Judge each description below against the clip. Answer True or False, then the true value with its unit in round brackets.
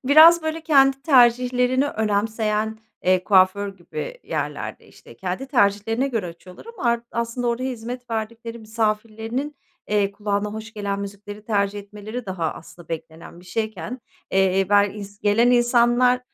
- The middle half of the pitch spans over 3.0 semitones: True (3.6 semitones)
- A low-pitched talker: False (220 Hz)